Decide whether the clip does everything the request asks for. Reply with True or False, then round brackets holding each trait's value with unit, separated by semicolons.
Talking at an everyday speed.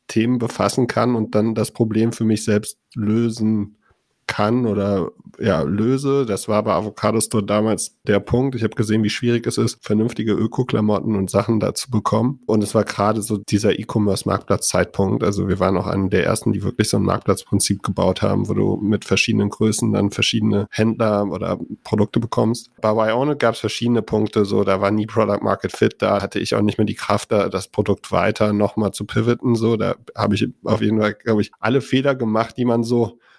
False (200 wpm)